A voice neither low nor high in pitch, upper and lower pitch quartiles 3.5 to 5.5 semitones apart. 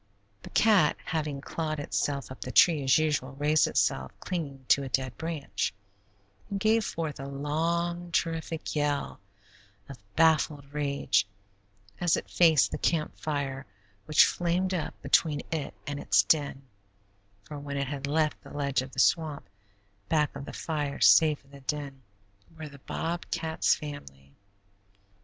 No: medium, 150 Hz; average, 2.7 semitones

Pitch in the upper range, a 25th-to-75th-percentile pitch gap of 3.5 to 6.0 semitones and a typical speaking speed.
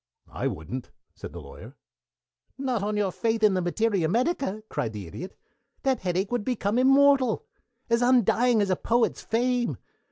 Yes: high, 225 Hz; average, 4.2 semitones; average, 160 wpm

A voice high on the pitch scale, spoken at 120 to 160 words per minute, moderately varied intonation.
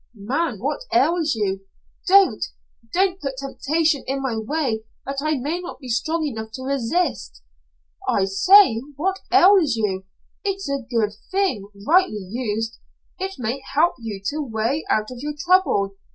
No: very high, 275 Hz; average, 155 wpm; wide, 7.2 semitones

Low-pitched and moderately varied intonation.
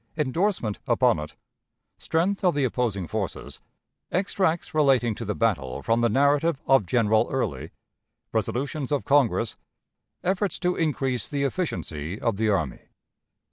No: low, 125 Hz; wide, 6.2 semitones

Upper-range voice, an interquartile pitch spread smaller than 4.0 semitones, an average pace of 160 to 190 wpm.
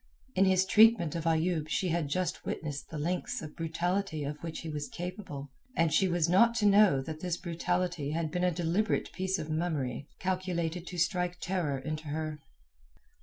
No: medium, 170 Hz; average, 2.9 semitones; average, 180 wpm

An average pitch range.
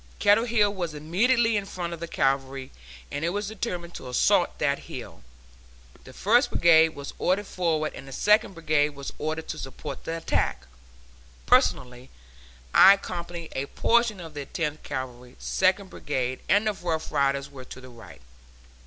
No: wide, 5.9 semitones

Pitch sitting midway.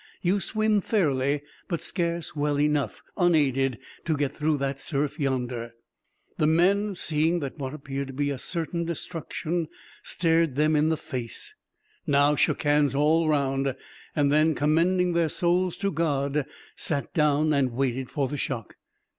Yes: medium, 150 Hz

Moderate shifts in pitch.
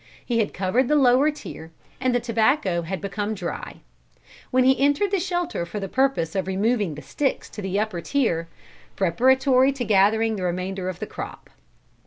No: wide, 5.9 semitones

